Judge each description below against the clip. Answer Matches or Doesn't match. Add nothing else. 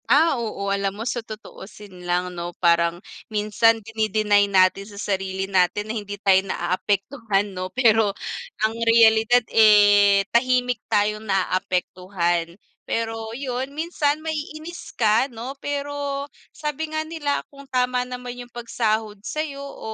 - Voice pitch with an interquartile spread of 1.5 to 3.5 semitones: Doesn't match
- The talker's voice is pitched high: Matches